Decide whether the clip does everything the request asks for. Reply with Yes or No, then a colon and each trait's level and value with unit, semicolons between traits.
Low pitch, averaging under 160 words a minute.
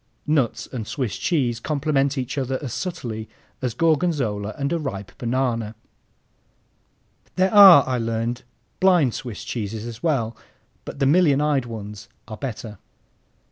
Yes: low, 130 Hz; average, 140 wpm